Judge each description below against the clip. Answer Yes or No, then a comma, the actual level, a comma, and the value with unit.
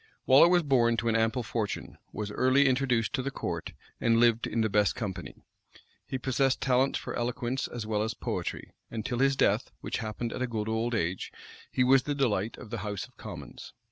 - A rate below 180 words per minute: No, fast, 205 wpm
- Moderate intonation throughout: Yes, average, 3.0 semitones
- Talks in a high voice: No, low, 120 Hz